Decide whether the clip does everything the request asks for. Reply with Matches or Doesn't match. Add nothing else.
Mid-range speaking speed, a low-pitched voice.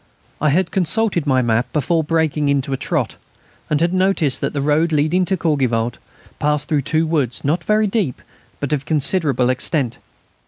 Doesn't match